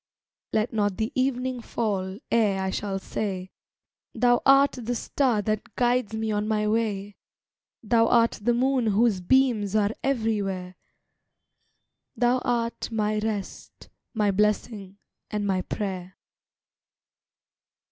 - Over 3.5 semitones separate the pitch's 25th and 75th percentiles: No, average, 3.1 semitones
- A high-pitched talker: Yes, high, 215 Hz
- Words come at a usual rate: No, slow, 120 wpm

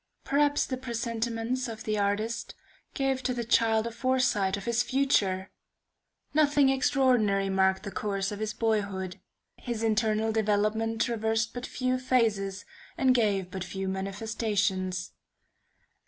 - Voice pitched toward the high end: Yes, high, 220 Hz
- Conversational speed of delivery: No, slow, 130 wpm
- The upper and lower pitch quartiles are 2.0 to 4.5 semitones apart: Yes, average, 3.7 semitones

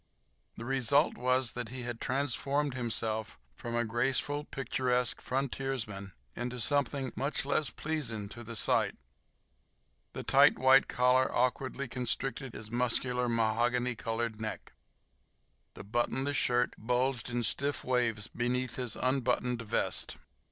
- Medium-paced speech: No, slow, 125 wpm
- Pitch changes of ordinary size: No, narrow, 2.2 semitones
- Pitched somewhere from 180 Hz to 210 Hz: No, low, 125 Hz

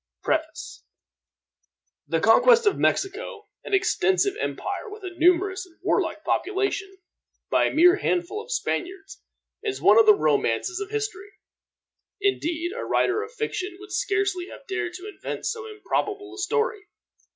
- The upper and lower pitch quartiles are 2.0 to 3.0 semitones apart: Yes, narrow, 2.5 semitones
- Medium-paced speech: Yes, average, 145 wpm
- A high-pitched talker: Yes, very high, 395 Hz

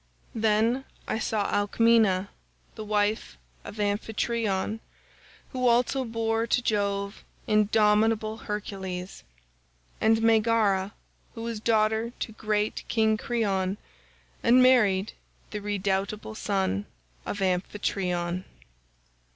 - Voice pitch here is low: No, high, 215 Hz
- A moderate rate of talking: No, slow, 95 wpm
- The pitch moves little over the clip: Yes, narrow, 2.1 semitones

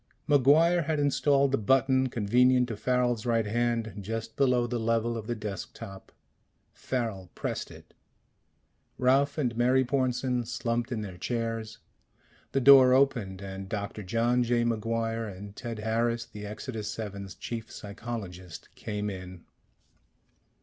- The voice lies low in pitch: Yes, low, 115 Hz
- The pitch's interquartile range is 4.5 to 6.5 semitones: No, average, 3.1 semitones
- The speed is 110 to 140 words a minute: Yes, slow, 135 wpm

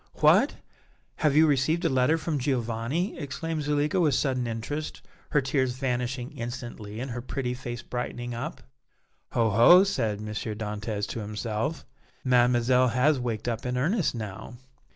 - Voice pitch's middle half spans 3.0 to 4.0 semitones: Yes, average, 3.7 semitones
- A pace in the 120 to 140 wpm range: No, average, 150 wpm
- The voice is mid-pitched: No, low, 125 Hz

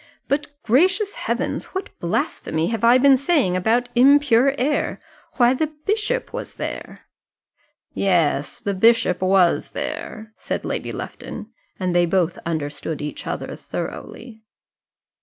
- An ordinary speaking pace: No, slow, 125 wpm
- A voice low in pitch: No, high, 230 Hz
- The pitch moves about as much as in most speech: No, wide, 7.6 semitones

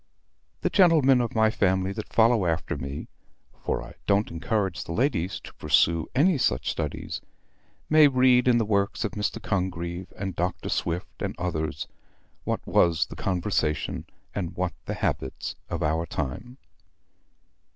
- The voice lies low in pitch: Yes, very low, 95 Hz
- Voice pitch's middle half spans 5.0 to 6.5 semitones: Yes, wide, 5.5 semitones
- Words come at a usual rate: Yes, average, 150 wpm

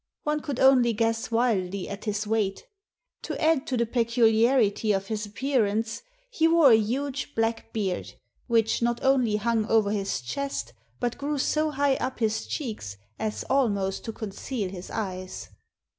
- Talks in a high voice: Yes, high, 225 Hz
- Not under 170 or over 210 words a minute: No, average, 160 wpm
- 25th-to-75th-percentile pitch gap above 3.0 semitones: Yes, average, 4.0 semitones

